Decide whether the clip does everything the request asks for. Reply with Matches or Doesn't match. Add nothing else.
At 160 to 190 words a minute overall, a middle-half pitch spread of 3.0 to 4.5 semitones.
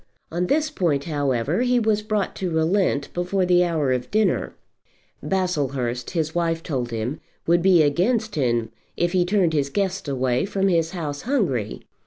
Doesn't match